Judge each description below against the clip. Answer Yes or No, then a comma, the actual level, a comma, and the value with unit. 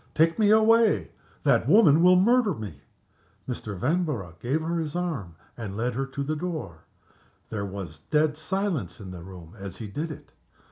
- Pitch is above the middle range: No, medium, 145 Hz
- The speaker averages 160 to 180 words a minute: Yes, average, 175 wpm